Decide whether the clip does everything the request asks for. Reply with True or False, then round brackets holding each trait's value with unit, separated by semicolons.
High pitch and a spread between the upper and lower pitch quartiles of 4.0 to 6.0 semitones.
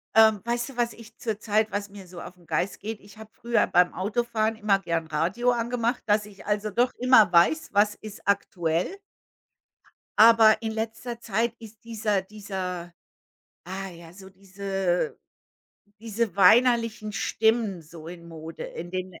False (210 Hz; 3.6 semitones)